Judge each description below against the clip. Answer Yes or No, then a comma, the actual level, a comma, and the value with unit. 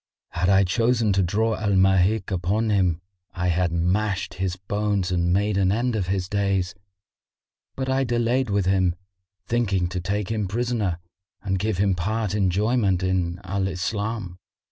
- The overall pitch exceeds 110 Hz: No, very low, 95 Hz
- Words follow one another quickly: No, average, 160 wpm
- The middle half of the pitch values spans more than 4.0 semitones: No, average, 2.8 semitones